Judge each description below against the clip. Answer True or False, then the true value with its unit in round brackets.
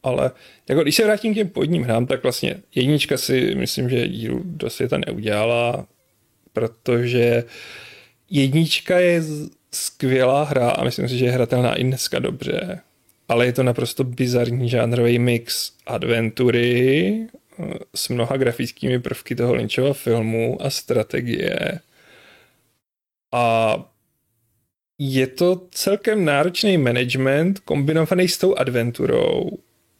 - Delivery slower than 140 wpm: True (120 wpm)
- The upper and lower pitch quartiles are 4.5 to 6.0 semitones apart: True (5.5 semitones)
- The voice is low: True (130 Hz)